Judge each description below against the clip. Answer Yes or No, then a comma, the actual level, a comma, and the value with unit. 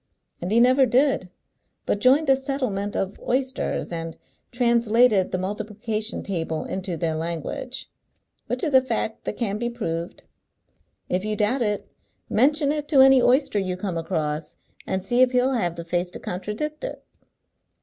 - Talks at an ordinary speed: Yes, average, 160 wpm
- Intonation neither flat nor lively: No, wide, 5.9 semitones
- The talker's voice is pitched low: No, high, 215 Hz